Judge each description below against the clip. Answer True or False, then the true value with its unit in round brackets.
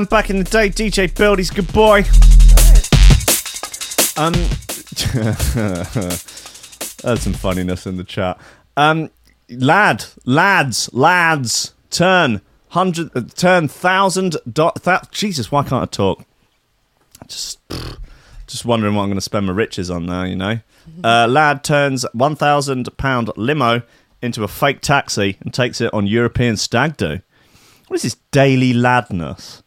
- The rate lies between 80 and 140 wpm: True (135 wpm)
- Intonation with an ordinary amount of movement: False (6.8 semitones)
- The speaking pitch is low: True (125 Hz)